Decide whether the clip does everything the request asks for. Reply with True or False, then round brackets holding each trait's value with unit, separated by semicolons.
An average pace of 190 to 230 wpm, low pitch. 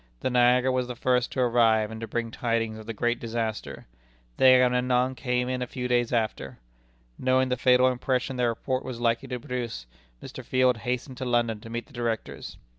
True (195 wpm; 125 Hz)